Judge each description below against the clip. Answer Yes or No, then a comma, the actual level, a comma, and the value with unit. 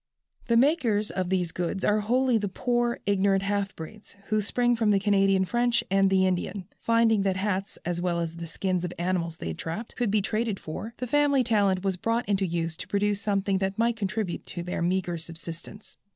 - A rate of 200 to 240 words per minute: Yes, fast, 205 wpm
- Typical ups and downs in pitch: Yes, average, 3.5 semitones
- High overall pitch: Yes, high, 195 Hz